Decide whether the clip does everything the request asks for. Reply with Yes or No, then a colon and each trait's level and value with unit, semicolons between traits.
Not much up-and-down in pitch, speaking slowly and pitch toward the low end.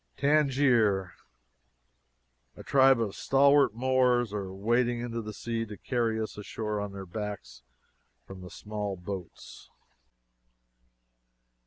No: average, 3.7 semitones; slow, 115 wpm; low, 110 Hz